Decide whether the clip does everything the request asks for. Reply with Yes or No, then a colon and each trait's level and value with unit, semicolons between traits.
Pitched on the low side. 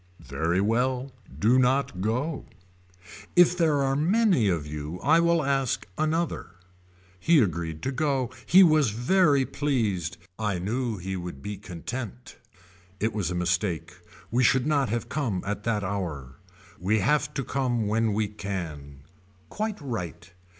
Yes: low, 115 Hz